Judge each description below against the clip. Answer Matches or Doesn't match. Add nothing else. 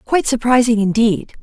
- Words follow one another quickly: Doesn't match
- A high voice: Matches